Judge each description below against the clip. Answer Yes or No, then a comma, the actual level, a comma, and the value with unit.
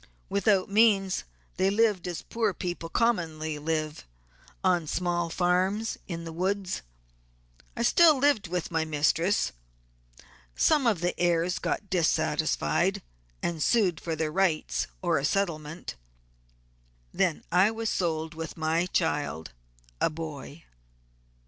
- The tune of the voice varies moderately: Yes, average, 3.7 semitones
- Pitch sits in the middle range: Yes, medium, 175 Hz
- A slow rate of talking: Yes, slow, 125 wpm